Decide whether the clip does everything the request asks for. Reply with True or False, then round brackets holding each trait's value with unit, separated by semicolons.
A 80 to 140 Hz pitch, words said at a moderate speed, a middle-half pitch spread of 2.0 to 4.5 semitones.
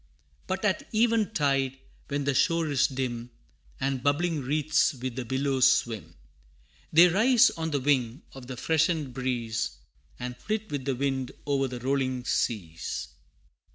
True (135 Hz; 150 wpm; 3.9 semitones)